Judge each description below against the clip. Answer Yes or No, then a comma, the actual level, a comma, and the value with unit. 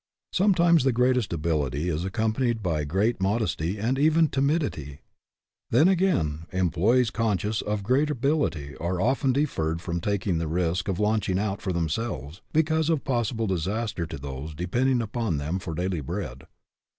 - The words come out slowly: No, average, 160 wpm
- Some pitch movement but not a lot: No, wide, 7.3 semitones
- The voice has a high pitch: No, low, 100 Hz